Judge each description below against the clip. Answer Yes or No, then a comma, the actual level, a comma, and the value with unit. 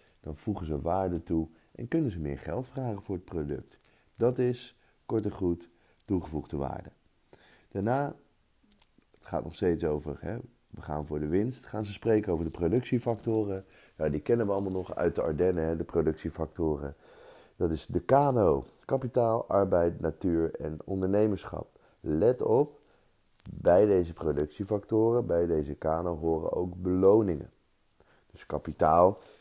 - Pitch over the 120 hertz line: No, very low, 95 Hz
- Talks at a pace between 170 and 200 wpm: No, average, 150 wpm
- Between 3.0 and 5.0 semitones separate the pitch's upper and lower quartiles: No, wide, 5.4 semitones